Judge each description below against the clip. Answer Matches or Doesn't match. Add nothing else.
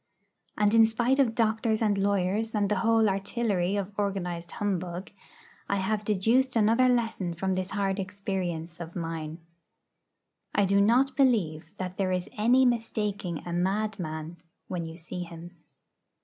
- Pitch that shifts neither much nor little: Matches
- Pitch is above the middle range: Matches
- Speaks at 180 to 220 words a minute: Doesn't match